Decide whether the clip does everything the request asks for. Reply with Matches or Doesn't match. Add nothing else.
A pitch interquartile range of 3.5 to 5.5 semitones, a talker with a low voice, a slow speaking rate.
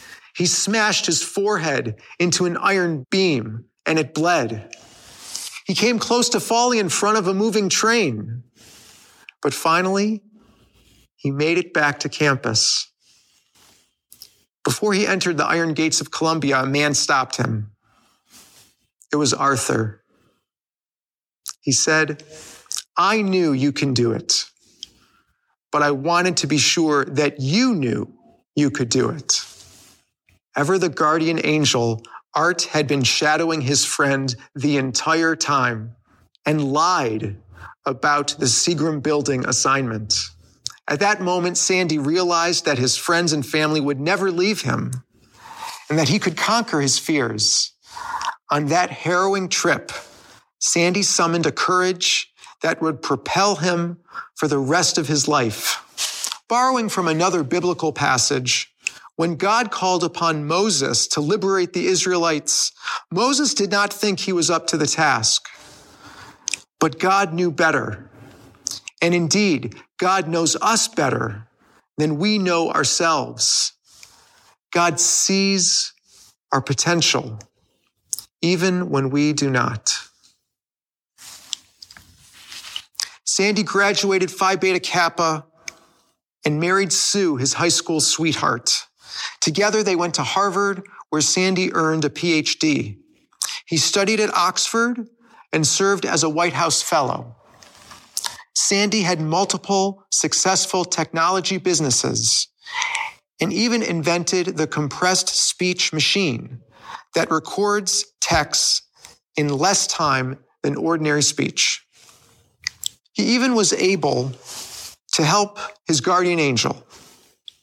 Doesn't match